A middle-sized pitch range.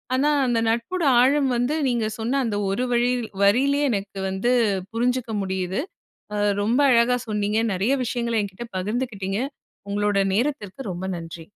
Yes: average, 3.8 semitones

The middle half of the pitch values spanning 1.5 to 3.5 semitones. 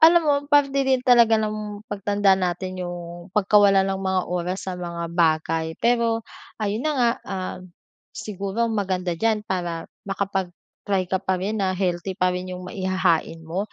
Yes: average, 3.0 semitones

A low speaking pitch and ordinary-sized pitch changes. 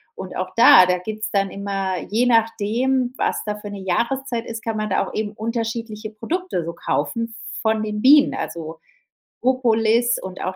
No: high, 220 Hz; average, 3.0 semitones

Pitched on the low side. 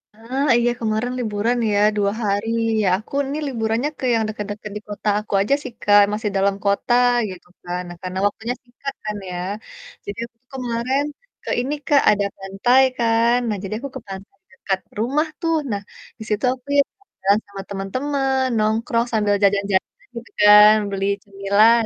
No: high, 215 Hz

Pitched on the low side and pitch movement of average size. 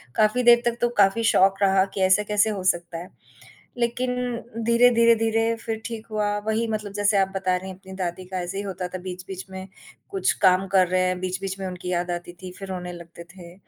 No: high, 195 Hz; average, 3.1 semitones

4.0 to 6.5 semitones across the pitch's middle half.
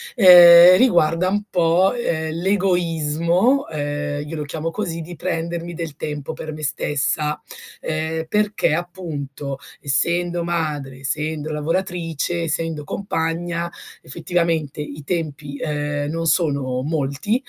No: average, 2.7 semitones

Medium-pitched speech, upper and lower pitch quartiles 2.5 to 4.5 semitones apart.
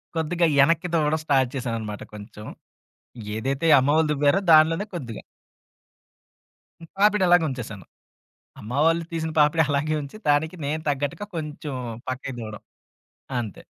Yes: medium, 145 Hz; average, 3.9 semitones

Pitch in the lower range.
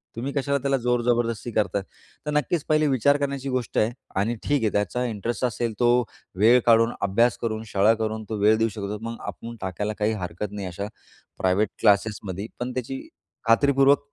Yes: low, 115 Hz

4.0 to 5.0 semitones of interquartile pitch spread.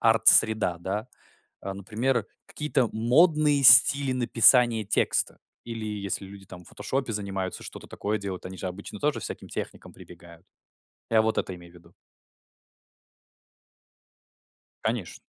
Yes: average, 4.3 semitones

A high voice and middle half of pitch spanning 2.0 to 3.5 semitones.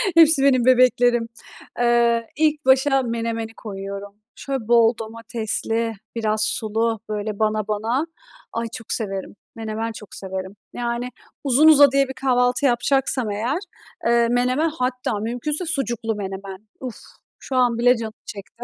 Yes: high, 235 Hz; average, 2.8 semitones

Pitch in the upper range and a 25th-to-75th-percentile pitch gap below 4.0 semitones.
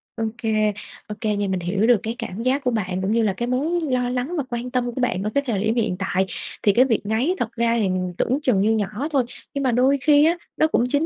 Yes: high, 235 Hz; average, 3.6 semitones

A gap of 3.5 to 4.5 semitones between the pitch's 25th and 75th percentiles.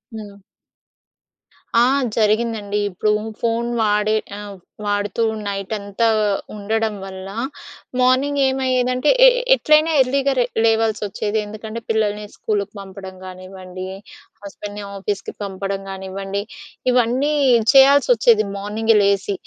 No: average, 2.8 semitones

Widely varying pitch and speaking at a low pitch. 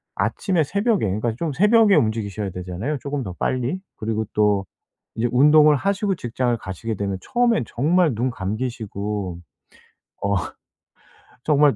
Yes: wide, 6.9 semitones; low, 120 Hz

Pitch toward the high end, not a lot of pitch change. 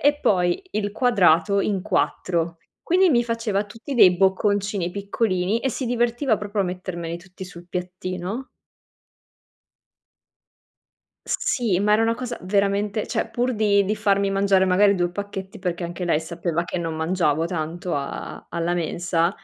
No: high, 195 Hz; average, 3.3 semitones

